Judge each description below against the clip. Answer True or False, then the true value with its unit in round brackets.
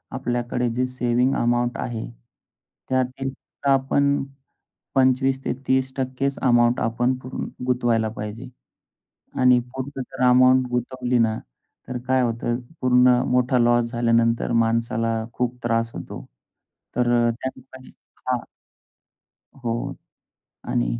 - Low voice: True (125 Hz)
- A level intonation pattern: True (1.6 semitones)